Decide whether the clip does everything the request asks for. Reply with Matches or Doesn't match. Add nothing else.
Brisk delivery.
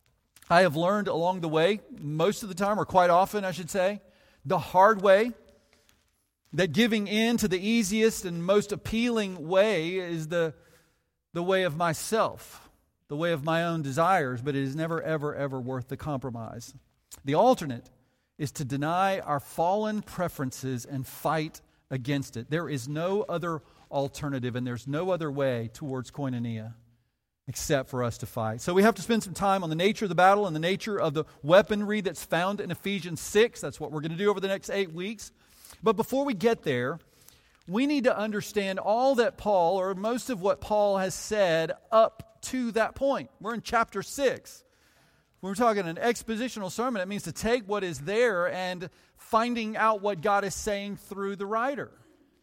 Doesn't match